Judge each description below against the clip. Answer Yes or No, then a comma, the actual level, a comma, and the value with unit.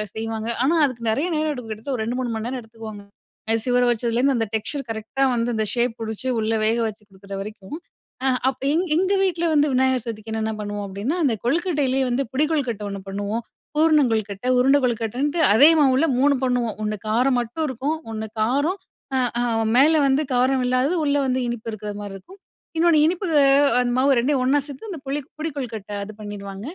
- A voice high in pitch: Yes, high, 245 Hz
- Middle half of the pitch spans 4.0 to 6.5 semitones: Yes, average, 4.3 semitones